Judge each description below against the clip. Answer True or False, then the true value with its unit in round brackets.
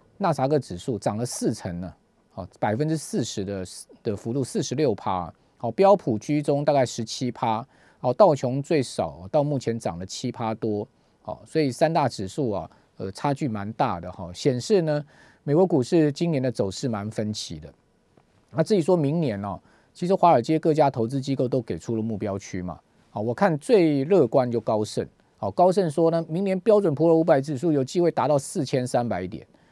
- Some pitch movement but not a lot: False (6.5 semitones)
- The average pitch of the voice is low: True (130 Hz)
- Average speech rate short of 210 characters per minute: False (280 characters per minute)